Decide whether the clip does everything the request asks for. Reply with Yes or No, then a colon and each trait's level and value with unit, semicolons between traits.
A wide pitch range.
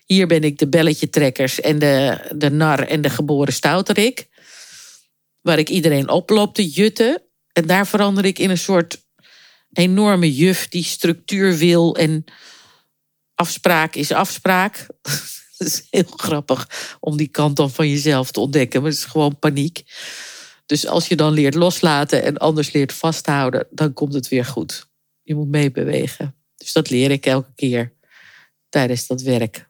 No: average, 3.5 semitones